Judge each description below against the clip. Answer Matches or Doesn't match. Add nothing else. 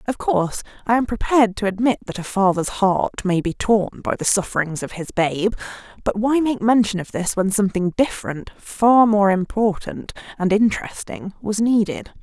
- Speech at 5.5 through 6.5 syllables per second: Doesn't match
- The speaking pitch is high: Matches